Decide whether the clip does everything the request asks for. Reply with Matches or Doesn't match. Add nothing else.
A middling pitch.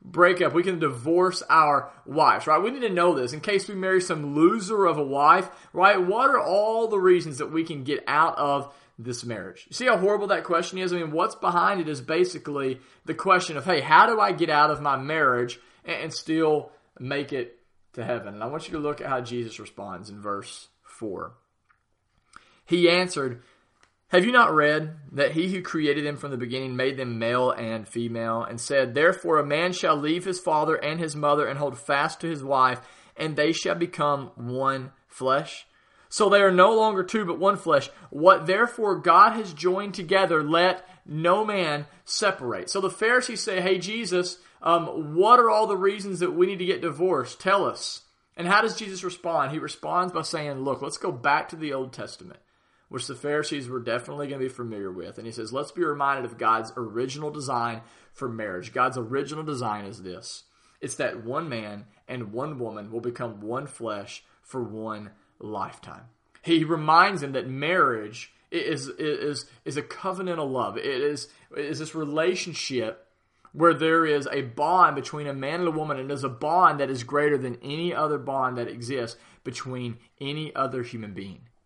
Matches